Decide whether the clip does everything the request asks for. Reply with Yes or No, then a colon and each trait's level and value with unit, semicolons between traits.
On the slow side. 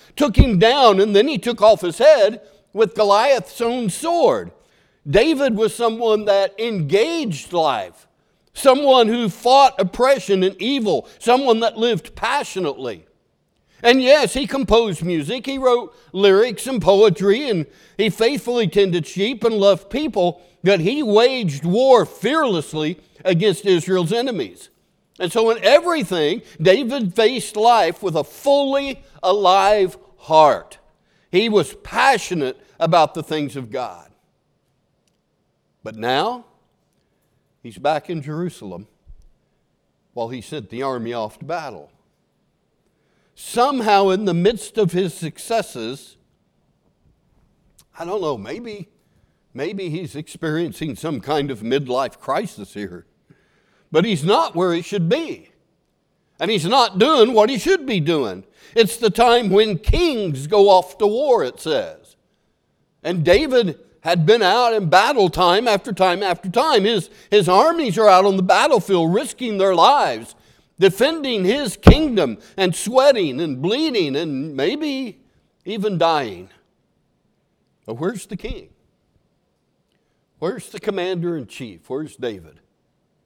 Yes: slow, 130 wpm